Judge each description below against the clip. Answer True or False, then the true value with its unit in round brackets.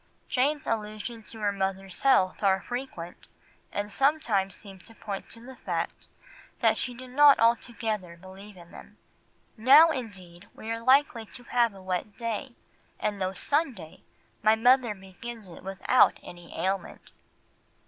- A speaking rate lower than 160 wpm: True (150 wpm)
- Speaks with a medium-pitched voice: False (215 Hz)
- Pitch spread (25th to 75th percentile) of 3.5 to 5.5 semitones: True (4.3 semitones)